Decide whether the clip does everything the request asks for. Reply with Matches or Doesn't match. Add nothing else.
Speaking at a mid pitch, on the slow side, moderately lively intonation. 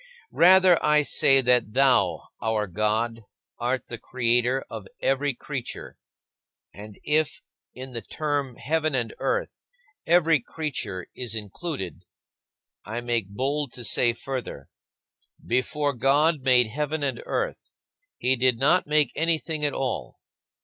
Doesn't match